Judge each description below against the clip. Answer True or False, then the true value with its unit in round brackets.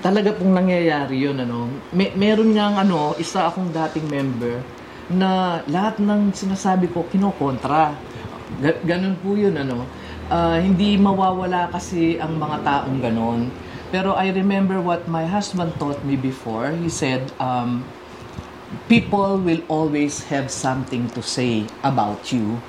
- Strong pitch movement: True (6.2 semitones)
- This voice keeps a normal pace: True (140 wpm)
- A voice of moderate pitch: True (165 Hz)